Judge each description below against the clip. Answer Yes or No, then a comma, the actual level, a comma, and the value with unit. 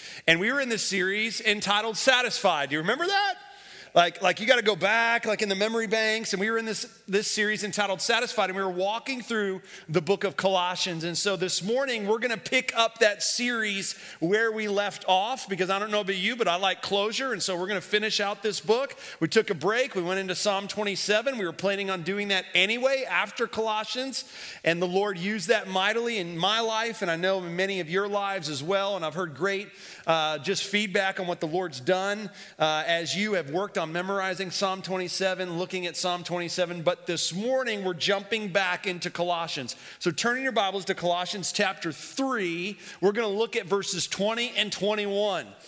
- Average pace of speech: No, fast, 215 wpm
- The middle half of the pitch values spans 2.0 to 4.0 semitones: Yes, average, 3.1 semitones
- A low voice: No, high, 200 Hz